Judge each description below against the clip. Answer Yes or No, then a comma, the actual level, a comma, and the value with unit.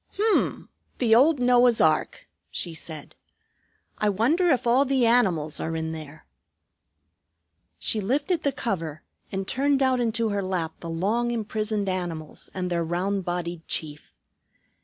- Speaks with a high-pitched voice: Yes, high, 205 Hz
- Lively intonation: Yes, wide, 6.7 semitones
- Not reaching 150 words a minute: Yes, average, 140 wpm